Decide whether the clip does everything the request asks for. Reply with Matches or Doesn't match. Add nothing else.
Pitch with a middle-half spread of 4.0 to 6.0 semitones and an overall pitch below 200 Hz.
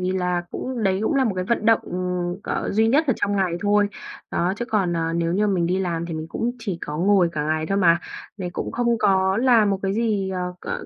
Doesn't match